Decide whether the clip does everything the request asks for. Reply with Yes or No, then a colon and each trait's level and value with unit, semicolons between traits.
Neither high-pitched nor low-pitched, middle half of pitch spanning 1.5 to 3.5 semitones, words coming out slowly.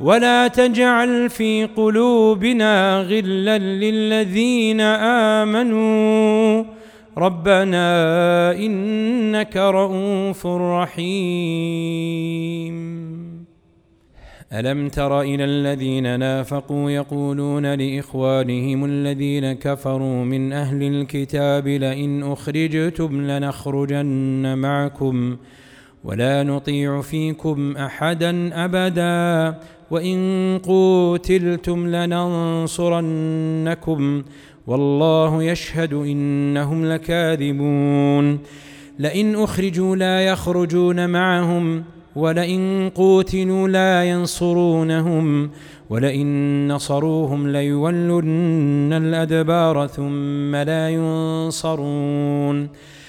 No: medium, 160 Hz; average, 4.5 semitones; slow, 60 wpm